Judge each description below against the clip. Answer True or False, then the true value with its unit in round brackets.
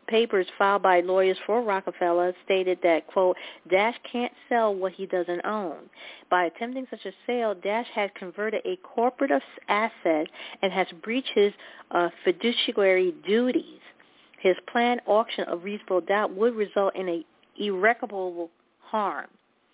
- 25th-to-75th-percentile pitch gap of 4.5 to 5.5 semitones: False (4.1 semitones)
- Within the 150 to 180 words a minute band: False (140 wpm)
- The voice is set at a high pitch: True (200 Hz)